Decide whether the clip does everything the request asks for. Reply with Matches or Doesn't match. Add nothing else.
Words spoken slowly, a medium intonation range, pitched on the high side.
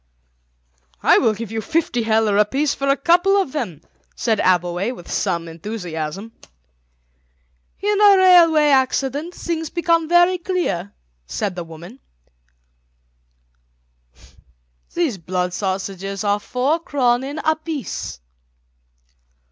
Doesn't match